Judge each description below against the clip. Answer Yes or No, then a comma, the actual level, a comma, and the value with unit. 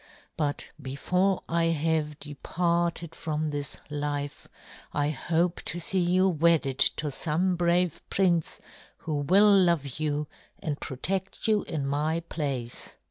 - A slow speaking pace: Yes, slow, 130 wpm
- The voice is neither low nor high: Yes, medium, 160 Hz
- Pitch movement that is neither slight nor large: Yes, average, 3.1 semitones